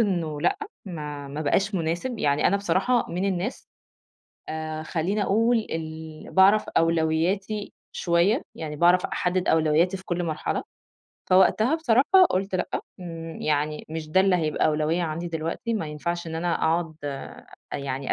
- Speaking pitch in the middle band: Yes, medium, 170 Hz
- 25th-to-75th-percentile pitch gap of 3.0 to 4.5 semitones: Yes, average, 3.5 semitones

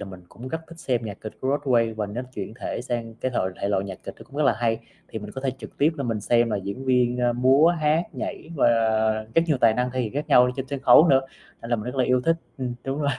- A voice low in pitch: Yes, low, 125 Hz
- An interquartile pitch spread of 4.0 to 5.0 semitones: No, average, 3.3 semitones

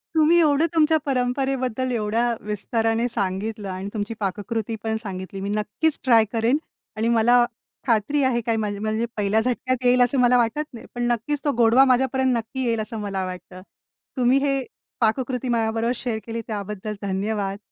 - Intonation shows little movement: No, average, 3.2 semitones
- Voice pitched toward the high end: Yes, high, 230 Hz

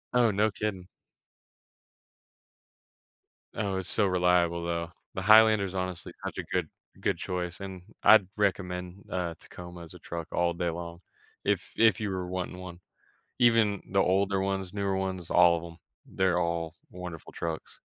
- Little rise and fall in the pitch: Yes, narrow, 2.1 semitones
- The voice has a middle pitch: No, very low, 90 Hz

